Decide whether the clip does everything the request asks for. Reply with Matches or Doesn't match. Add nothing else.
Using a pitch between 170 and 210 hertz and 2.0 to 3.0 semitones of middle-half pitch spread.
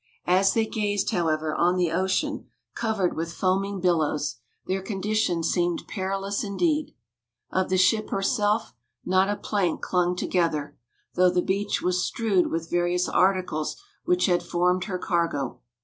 Matches